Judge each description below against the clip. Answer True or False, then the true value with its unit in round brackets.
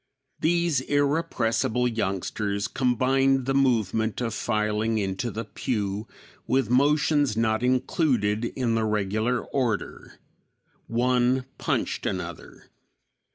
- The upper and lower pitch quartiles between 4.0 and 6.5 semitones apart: False (3.5 semitones)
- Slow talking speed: True (100 wpm)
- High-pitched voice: False (120 Hz)